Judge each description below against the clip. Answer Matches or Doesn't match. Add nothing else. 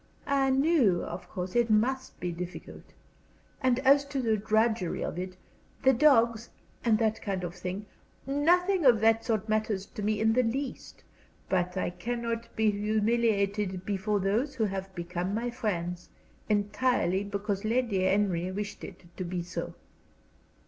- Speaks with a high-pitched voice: Matches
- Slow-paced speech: Doesn't match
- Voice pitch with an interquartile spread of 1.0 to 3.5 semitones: Doesn't match